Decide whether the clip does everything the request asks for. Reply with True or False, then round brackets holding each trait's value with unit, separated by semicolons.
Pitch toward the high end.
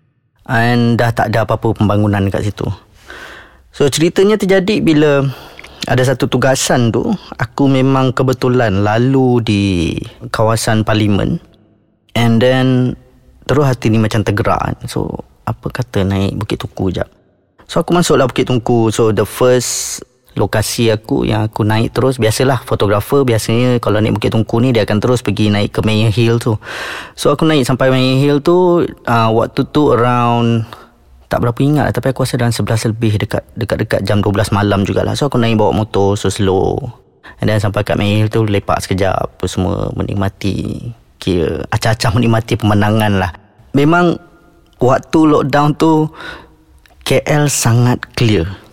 False (115 Hz)